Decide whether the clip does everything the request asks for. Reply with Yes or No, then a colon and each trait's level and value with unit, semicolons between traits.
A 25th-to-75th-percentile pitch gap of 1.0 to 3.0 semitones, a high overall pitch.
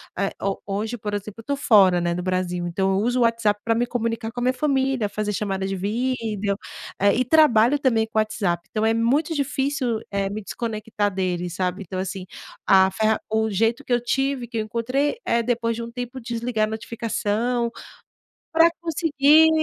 No: average, 3.6 semitones; high, 225 Hz